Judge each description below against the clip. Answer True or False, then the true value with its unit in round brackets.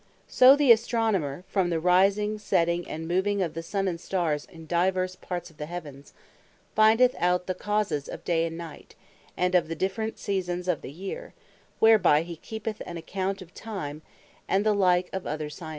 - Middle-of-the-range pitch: True (180 Hz)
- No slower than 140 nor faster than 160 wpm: False (185 wpm)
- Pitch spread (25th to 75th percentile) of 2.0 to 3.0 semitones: False (3.5 semitones)